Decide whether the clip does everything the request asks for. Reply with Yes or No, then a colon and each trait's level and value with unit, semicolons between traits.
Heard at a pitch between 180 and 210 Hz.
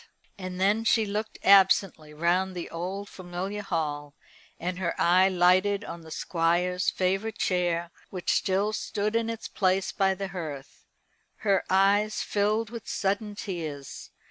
Yes: high, 190 Hz